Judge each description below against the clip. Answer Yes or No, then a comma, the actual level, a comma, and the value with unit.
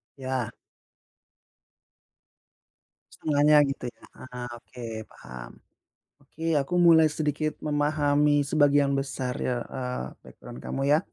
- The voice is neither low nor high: Yes, medium, 145 Hz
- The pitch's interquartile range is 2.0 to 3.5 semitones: Yes, average, 2.9 semitones